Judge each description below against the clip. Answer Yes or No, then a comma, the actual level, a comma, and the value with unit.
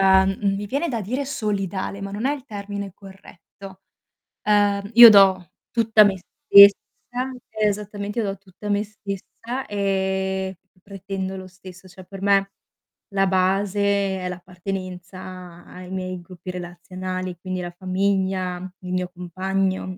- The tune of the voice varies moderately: No, narrow, 1.6 semitones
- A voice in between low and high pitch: No, high, 195 Hz